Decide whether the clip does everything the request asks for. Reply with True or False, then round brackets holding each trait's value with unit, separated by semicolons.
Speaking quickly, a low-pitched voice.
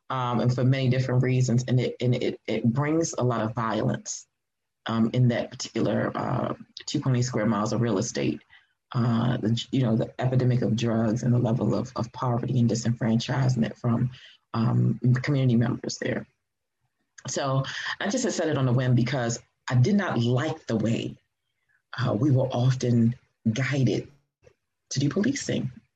False (165 wpm; 125 Hz)